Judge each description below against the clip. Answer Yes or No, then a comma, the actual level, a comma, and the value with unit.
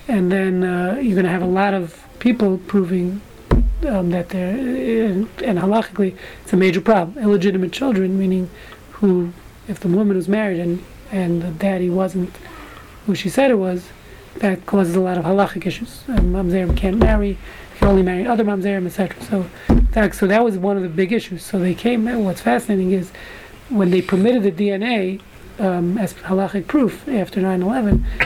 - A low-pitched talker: No, high, 195 Hz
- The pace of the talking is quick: No, average, 185 wpm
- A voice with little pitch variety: Yes, narrow, 2.2 semitones